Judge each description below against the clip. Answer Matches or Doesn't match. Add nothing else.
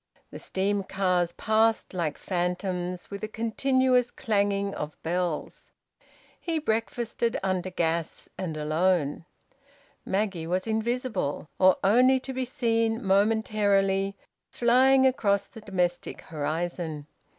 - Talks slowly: Matches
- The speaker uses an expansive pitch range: Doesn't match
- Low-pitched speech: Doesn't match